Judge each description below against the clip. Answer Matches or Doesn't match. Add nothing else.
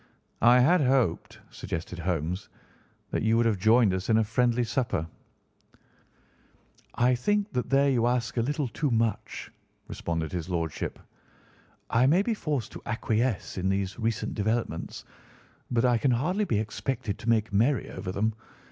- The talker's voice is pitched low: Matches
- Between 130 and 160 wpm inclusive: Matches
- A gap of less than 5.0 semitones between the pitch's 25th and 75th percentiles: Matches